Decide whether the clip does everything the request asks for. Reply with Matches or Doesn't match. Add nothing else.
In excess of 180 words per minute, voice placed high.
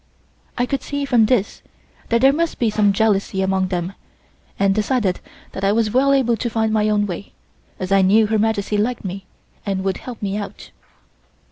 Matches